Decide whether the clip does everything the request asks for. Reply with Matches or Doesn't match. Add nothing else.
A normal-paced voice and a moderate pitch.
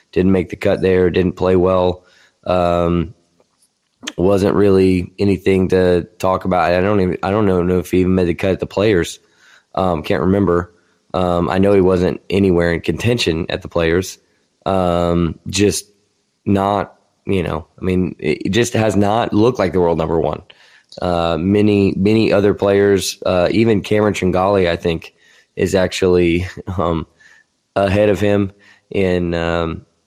Doesn't match